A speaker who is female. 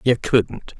No: male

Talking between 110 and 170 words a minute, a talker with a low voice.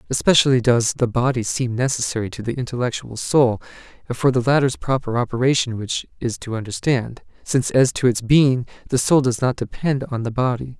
No: average, 180 wpm; low, 125 Hz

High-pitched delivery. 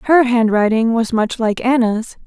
Yes: high, 230 Hz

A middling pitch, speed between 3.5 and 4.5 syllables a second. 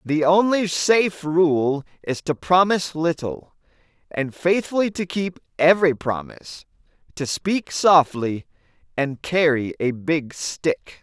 Yes: medium, 160 Hz; 3.9 syllables/s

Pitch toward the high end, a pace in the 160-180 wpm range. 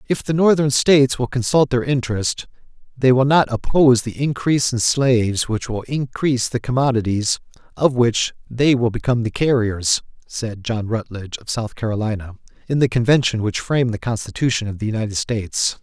No: low, 120 Hz; average, 170 wpm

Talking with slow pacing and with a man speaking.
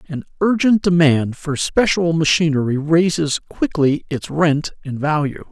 Yes: slow, 130 wpm; male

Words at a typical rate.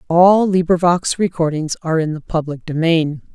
Yes: average, 145 wpm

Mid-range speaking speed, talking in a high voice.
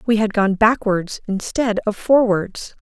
Yes: average, 150 wpm; high, 210 Hz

